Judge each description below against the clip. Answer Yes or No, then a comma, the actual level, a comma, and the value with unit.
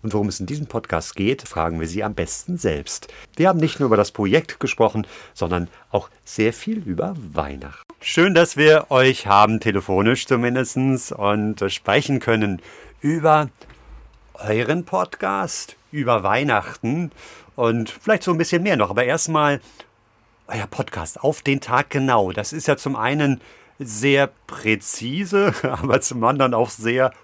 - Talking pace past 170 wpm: No, average, 150 wpm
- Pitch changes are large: Yes, wide, 5.8 semitones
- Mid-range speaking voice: No, low, 120 Hz